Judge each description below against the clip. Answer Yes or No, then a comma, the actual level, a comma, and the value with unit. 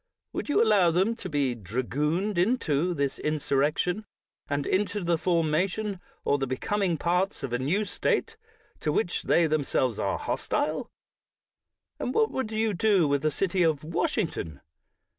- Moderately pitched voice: Yes, medium, 170 Hz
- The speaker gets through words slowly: No, average, 155 wpm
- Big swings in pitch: Yes, wide, 5.8 semitones